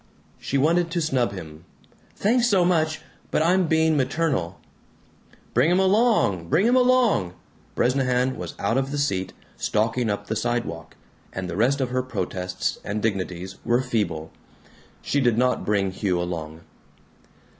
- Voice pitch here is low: Yes, low, 125 Hz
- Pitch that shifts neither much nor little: No, wide, 8.8 semitones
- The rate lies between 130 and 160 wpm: Yes, average, 150 wpm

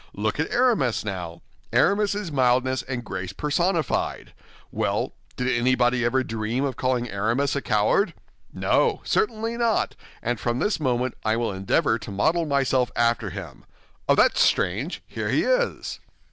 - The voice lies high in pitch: No, low, 125 Hz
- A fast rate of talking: No, average, 150 wpm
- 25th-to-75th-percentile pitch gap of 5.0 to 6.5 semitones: Yes, average, 5.3 semitones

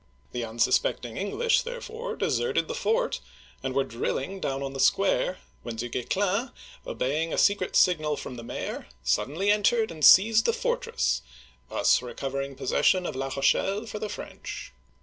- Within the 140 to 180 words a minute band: Yes, average, 160 wpm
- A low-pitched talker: No, medium, 185 Hz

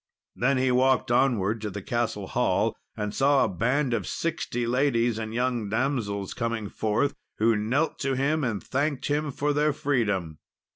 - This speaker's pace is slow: No, average, 165 wpm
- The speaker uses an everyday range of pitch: Yes, average, 4.1 semitones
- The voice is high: No, low, 120 Hz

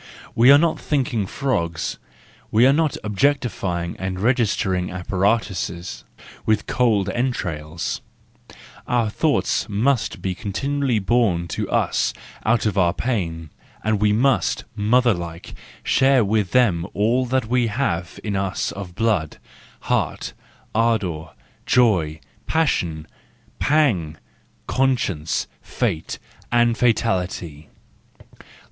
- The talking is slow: Yes, slow, 105 wpm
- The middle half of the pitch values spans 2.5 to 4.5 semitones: No, wide, 5.6 semitones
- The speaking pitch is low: Yes, low, 105 Hz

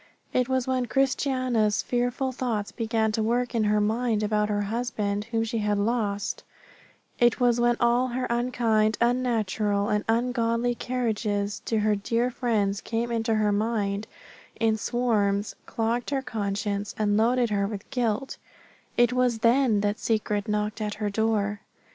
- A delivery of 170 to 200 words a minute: No, average, 155 wpm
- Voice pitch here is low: No, high, 225 Hz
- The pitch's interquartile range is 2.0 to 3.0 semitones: Yes, narrow, 2.6 semitones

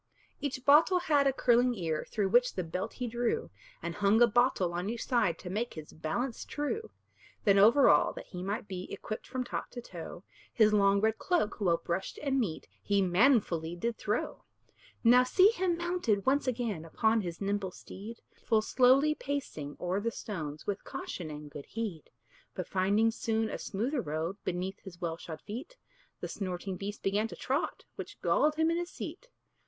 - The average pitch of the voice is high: Yes, high, 215 Hz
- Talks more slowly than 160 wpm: No, average, 185 wpm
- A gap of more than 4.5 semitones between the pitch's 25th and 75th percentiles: Yes, wide, 5.6 semitones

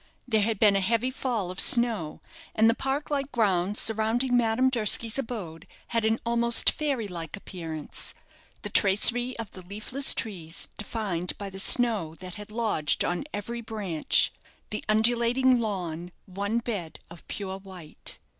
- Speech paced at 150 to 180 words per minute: Yes, average, 155 wpm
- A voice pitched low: No, high, 215 Hz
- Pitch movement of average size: Yes, average, 4.0 semitones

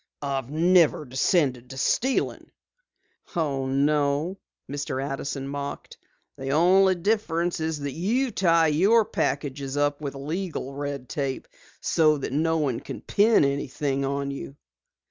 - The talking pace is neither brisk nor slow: No, slow, 125 wpm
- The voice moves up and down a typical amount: Yes, average, 3.5 semitones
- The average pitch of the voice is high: No, medium, 145 Hz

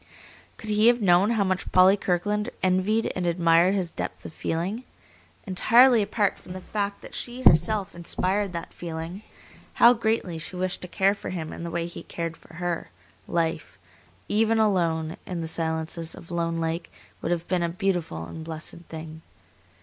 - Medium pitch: Yes, medium, 180 Hz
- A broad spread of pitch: No, average, 3.5 semitones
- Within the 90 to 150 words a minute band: No, average, 175 wpm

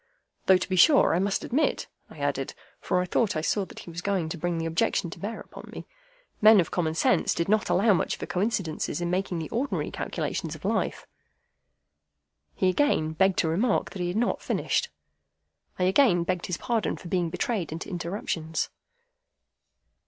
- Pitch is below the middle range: No, medium, 180 Hz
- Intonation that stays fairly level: No, average, 3.6 semitones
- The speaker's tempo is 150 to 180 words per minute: No, average, 190 wpm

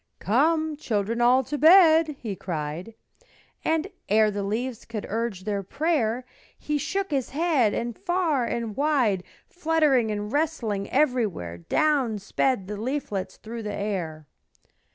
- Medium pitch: No, high, 235 Hz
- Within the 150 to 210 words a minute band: No, slow, 135 wpm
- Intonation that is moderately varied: No, wide, 6.6 semitones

